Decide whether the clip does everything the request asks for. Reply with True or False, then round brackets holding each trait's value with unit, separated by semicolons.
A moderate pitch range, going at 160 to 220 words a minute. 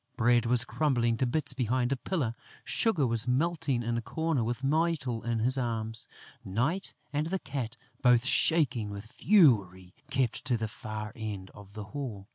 True (4.0 semitones; 170 wpm)